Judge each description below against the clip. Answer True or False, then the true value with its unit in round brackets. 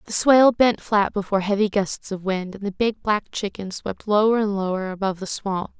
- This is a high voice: True (200 Hz)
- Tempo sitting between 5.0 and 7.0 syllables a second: True (5.4 syllables/s)